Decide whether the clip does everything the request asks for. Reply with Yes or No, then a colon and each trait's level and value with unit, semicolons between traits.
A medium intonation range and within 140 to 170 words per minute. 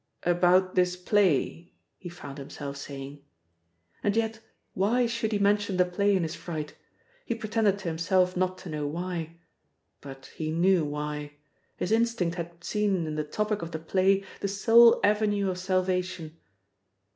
Yes: average, 3.9 semitones; average, 155 wpm